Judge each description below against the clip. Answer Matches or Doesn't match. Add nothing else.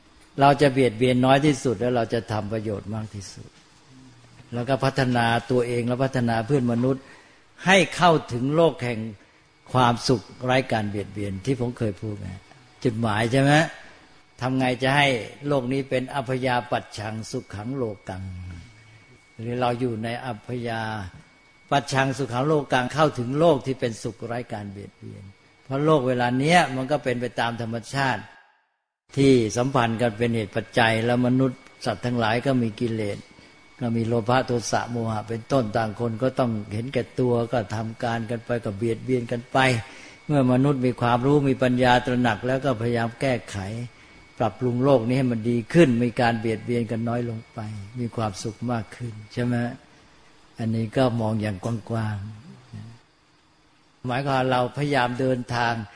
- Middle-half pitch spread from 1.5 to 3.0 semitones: Matches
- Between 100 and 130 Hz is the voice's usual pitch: Matches